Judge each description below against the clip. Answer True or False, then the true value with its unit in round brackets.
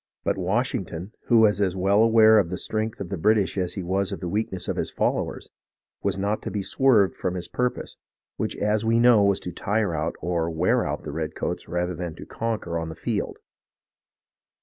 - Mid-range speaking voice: False (95 Hz)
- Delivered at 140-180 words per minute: False (205 wpm)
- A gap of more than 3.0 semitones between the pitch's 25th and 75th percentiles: True (3.7 semitones)